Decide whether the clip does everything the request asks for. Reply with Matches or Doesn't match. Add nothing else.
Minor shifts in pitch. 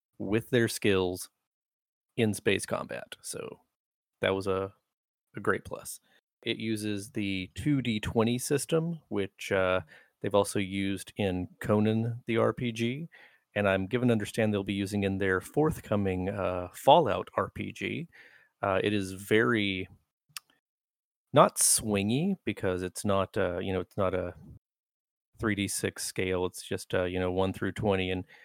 Doesn't match